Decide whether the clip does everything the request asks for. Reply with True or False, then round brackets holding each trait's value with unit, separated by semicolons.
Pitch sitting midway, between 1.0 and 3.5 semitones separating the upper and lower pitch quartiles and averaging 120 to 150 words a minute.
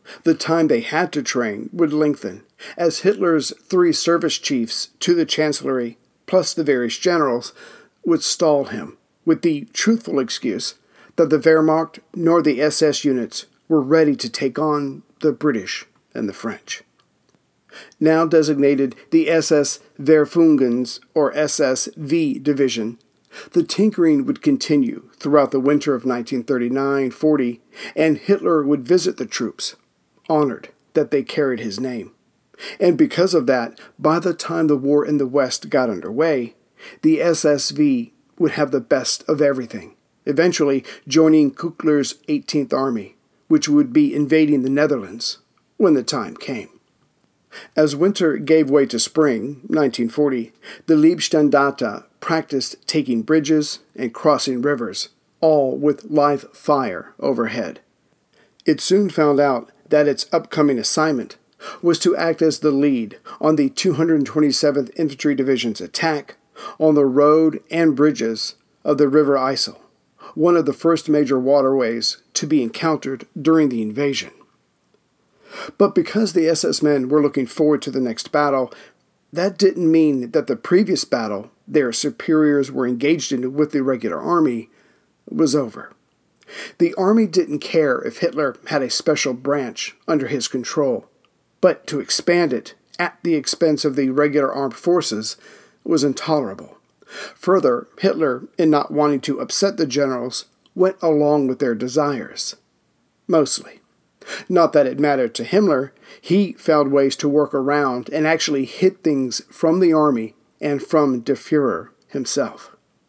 True (150 Hz; 3.2 semitones; 140 wpm)